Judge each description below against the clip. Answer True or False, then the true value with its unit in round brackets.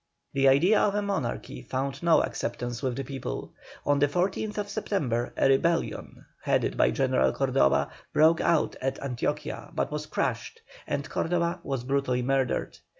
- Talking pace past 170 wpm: False (150 wpm)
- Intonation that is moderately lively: True (4.9 semitones)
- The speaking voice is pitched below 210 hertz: True (140 Hz)